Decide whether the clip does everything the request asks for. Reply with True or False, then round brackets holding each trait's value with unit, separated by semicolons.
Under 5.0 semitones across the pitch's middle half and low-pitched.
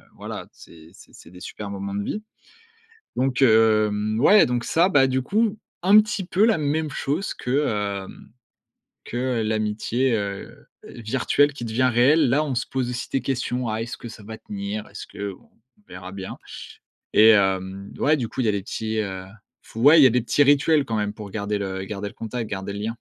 False (5.3 semitones; 115 Hz)